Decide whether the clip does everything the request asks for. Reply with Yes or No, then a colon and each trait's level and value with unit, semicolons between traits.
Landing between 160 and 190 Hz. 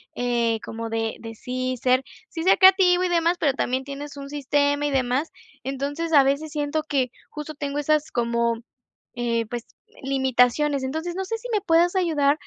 No: very high, 280 Hz